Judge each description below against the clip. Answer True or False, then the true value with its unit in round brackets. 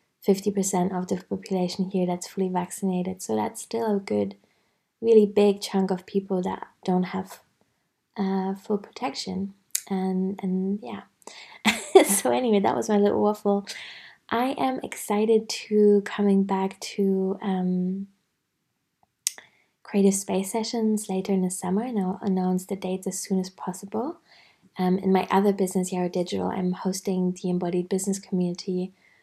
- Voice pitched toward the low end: False (195 Hz)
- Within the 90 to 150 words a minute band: True (145 wpm)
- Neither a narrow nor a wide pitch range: False (1.8 semitones)